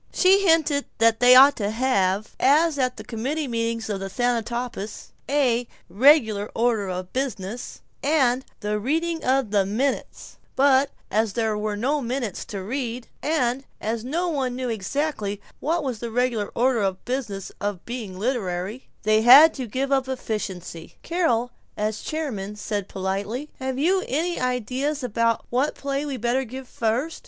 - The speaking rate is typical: Yes, average, 160 wpm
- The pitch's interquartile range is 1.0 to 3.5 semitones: No, average, 4.4 semitones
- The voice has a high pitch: Yes, high, 245 Hz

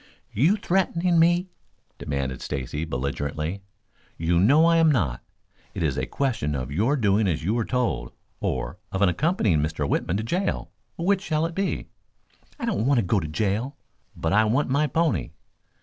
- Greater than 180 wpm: No, average, 170 wpm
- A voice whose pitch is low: Yes, low, 110 Hz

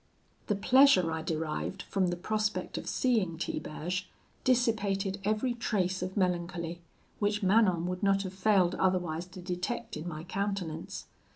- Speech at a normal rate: Yes, average, 145 wpm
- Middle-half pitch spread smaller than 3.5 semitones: Yes, average, 3.0 semitones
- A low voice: No, medium, 185 Hz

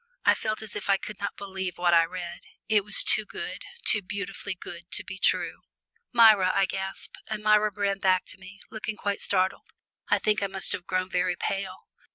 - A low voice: No, high, 195 Hz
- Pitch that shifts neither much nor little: No, narrow, 2.1 semitones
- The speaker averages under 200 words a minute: No, fast, 205 wpm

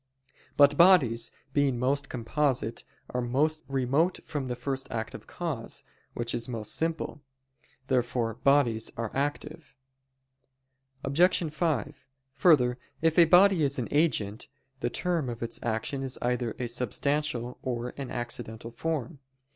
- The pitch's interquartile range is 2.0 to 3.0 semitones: No, average, 3.9 semitones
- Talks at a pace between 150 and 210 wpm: No, slow, 135 wpm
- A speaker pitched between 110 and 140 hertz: Yes, low, 135 Hz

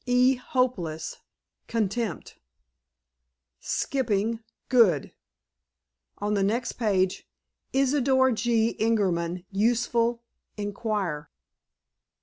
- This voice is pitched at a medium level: No, high, 225 Hz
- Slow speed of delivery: Yes, slow, 65 wpm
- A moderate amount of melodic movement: Yes, average, 3.8 semitones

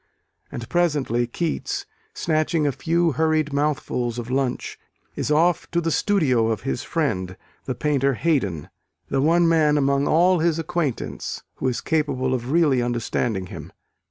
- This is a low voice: No, medium, 145 Hz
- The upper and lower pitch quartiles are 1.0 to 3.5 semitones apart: No, average, 4.9 semitones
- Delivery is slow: No, average, 150 wpm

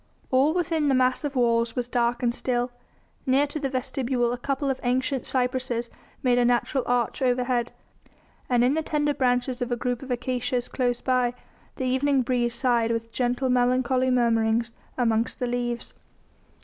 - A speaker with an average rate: Yes, average, 165 wpm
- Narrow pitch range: Yes, narrow, 1.3 semitones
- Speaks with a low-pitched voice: No, very high, 250 Hz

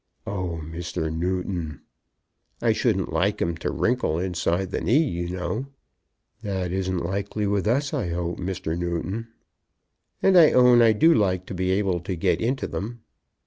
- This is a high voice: No, very low, 95 Hz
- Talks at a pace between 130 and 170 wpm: Yes, average, 160 wpm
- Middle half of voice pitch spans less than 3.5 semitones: No, average, 4.0 semitones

